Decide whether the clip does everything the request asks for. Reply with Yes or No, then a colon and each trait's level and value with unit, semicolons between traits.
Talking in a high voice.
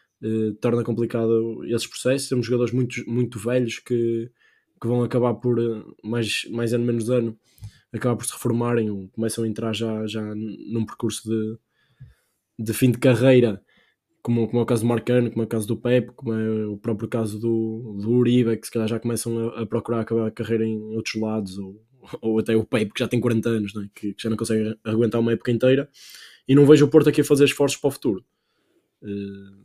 No: low, 115 Hz